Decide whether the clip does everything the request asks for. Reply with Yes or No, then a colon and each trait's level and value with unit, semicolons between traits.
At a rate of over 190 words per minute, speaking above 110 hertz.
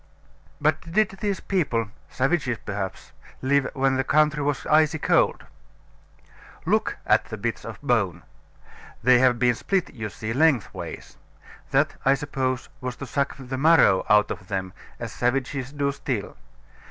No: average, 145 wpm; low, 135 Hz